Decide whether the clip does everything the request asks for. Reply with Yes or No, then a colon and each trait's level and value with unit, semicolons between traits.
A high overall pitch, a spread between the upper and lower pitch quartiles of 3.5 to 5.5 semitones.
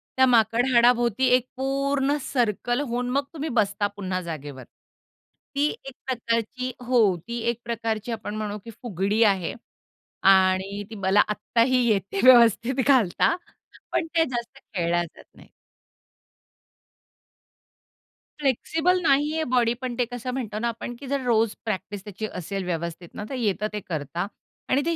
Yes: high, 230 Hz; average, 4.0 semitones